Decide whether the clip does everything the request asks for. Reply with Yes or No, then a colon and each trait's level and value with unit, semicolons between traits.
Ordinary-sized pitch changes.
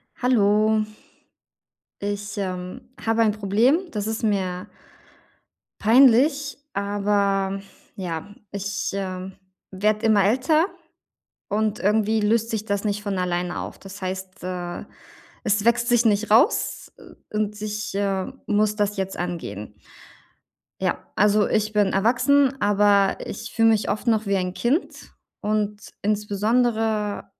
No: narrow, 2.0 semitones